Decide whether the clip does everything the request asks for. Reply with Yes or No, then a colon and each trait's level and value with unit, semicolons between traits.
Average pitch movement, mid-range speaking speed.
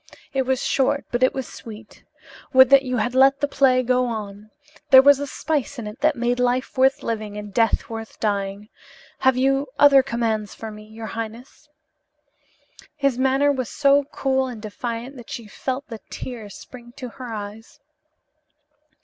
Yes: average, 3.2 semitones; average, 175 wpm